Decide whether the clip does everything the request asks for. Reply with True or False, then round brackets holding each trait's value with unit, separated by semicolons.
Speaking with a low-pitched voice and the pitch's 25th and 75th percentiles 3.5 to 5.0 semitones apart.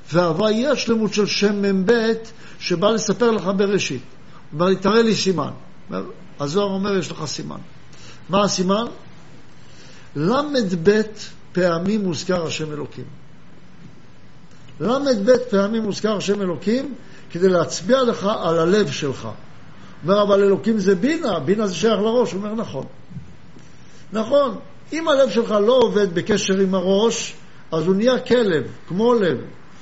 False (200 Hz; 4.3 semitones)